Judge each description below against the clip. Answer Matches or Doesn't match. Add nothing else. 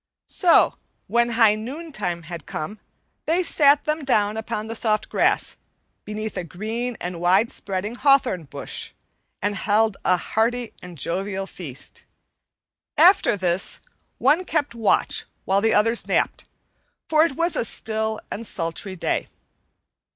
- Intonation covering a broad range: Doesn't match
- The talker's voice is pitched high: Matches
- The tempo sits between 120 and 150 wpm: Matches